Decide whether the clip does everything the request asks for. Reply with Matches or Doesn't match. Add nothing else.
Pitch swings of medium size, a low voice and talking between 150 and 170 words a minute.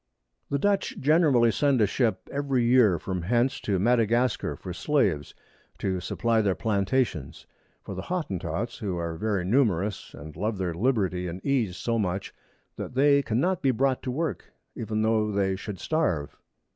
Doesn't match